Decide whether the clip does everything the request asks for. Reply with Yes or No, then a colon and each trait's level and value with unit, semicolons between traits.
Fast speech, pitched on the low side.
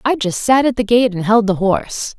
No: fast, 275 wpm; high, 220 Hz